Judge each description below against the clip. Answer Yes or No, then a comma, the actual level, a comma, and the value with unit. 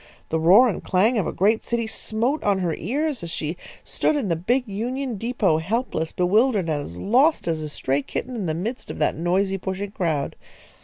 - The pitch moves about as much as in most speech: No, wide, 6.2 semitones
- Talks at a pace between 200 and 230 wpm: Yes, fast, 205 wpm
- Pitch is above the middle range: Yes, high, 195 Hz